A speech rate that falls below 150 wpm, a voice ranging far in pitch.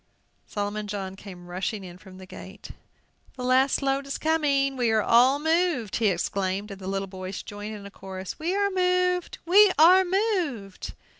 No: average, 175 wpm; wide, 8.6 semitones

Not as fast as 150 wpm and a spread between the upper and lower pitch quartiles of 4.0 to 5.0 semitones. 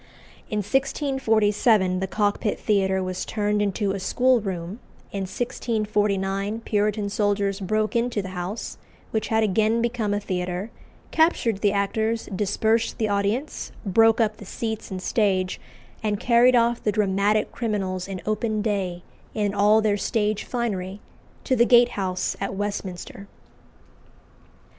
No: slow, 135 wpm; narrow, 2.4 semitones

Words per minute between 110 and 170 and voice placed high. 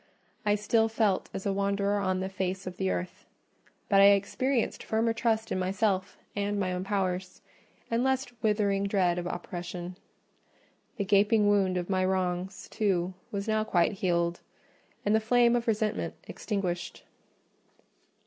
Yes: average, 150 wpm; high, 200 Hz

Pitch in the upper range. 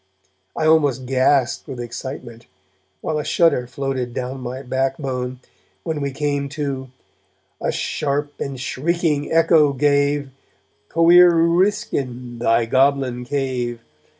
No: low, 135 Hz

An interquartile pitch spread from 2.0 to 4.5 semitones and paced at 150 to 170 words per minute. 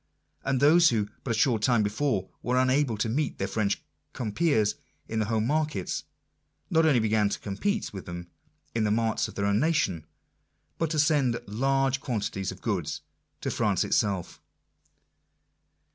No: average, 5.3 semitones; average, 160 wpm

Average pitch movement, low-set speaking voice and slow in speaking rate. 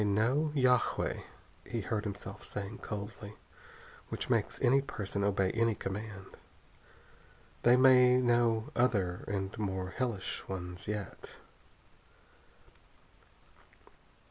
Yes: average, 3.6 semitones; low, 105 Hz; slow, 100 wpm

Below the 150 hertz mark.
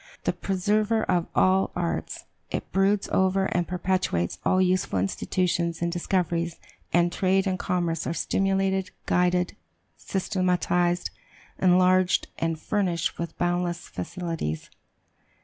No: medium, 180 Hz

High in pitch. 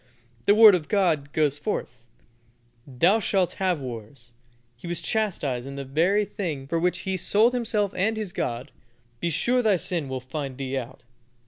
No: medium, 165 Hz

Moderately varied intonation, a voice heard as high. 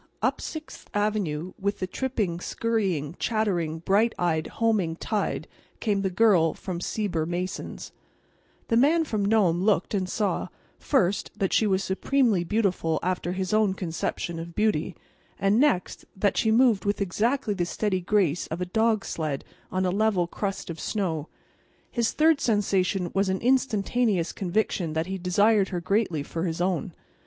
Yes: average, 3.7 semitones; high, 195 Hz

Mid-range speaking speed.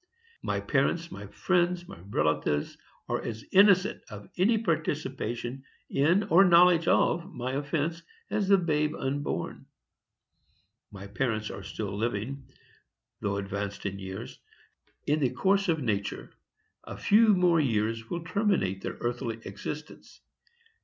No: slow, 130 wpm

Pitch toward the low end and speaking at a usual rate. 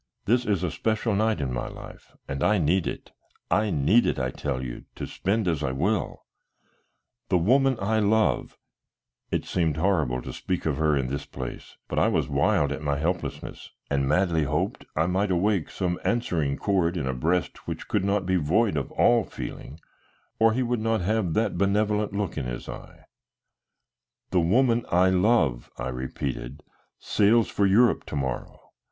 Yes: very low, 90 Hz; average, 180 wpm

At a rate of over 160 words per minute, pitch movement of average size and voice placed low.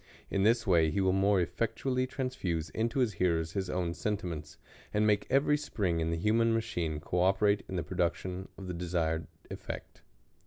Yes: average, 180 wpm; average, 4.5 semitones; very low, 95 Hz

